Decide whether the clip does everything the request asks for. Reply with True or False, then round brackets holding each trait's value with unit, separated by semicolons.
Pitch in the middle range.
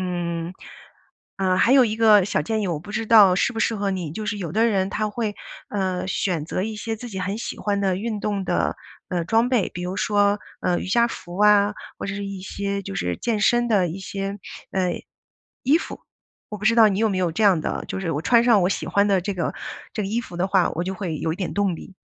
False (200 Hz)